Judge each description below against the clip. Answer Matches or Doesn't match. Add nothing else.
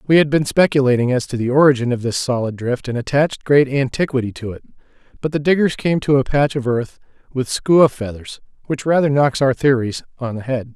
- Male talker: Matches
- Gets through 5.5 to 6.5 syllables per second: Matches